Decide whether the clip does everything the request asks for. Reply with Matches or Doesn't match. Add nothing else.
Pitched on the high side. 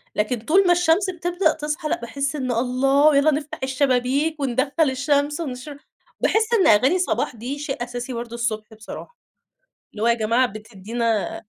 Matches